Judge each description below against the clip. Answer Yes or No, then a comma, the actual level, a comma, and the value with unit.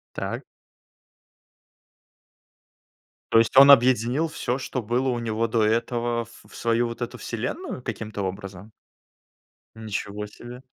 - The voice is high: No, low, 115 Hz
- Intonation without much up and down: Yes, narrow, 2.1 semitones